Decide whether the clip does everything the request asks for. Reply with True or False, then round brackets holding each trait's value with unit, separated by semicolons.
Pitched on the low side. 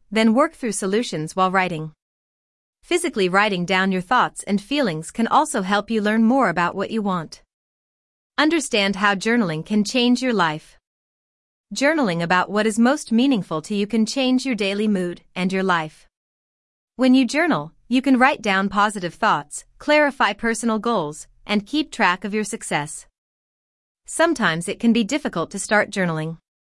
False (210 Hz)